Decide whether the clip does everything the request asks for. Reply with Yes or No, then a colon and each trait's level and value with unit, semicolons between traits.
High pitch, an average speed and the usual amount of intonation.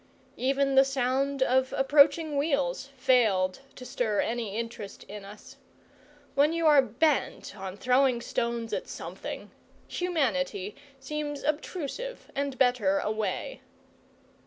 No: very high, 260 Hz; slow, 115 wpm; average, 4.0 semitones